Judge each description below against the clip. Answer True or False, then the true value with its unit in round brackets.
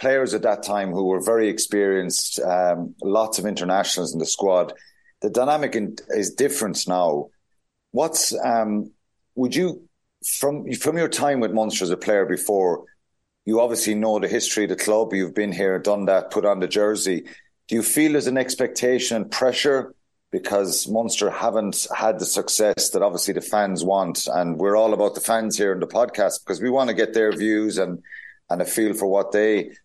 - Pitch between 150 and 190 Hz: False (110 Hz)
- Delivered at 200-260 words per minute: False (190 wpm)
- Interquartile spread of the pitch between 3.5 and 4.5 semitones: True (4.2 semitones)